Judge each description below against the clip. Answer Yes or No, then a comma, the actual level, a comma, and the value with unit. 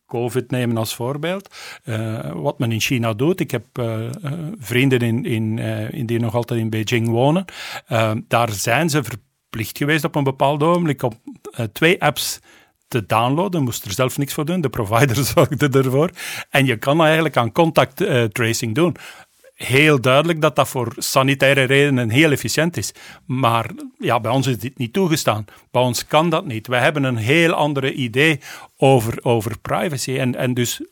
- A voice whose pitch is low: Yes, low, 130 Hz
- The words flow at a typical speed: Yes, average, 175 wpm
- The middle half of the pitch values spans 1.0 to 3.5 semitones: No, average, 4.3 semitones